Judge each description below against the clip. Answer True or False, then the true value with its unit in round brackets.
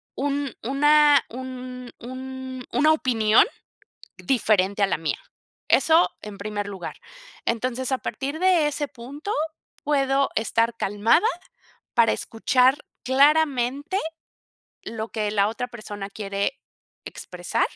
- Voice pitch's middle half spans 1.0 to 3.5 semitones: False (4.4 semitones)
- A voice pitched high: True (255 Hz)